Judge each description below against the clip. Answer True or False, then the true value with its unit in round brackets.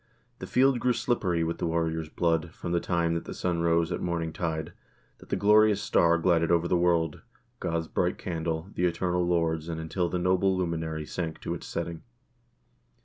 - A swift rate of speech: False (185 wpm)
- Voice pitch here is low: True (85 Hz)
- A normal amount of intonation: False (1.5 semitones)